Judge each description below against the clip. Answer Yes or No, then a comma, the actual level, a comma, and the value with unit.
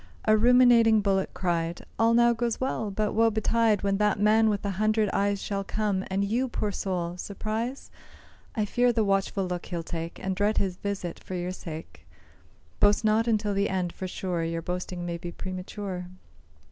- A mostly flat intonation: No, average, 3.0 semitones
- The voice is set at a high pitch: Yes, high, 200 Hz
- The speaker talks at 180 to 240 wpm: Yes, average, 185 wpm